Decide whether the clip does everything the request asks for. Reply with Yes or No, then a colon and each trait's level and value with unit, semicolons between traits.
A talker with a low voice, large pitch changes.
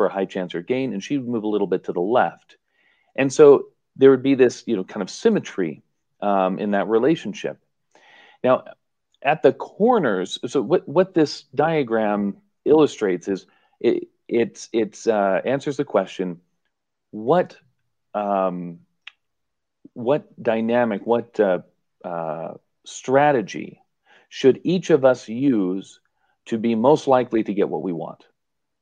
Yes: low, 120 Hz; wide, 6.5 semitones